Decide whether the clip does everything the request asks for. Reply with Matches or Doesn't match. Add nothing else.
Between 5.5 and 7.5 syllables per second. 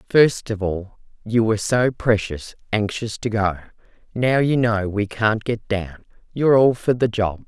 Doesn't match